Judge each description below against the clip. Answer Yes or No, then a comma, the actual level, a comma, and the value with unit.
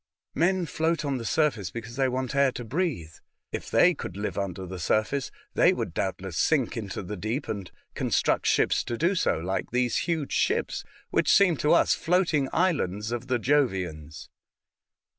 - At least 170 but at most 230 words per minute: Yes, average, 180 wpm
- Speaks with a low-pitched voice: Yes, low, 120 Hz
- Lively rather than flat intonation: Yes, wide, 7.7 semitones